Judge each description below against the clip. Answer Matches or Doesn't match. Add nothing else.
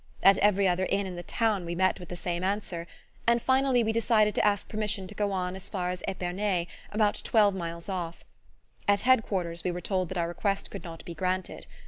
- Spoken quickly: Matches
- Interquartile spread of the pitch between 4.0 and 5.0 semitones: Doesn't match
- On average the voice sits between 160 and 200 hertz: Matches